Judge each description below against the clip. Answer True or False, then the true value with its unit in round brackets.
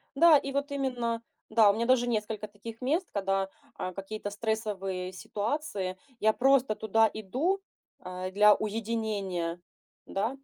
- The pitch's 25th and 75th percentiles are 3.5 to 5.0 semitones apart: True (4.0 semitones)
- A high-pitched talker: True (220 Hz)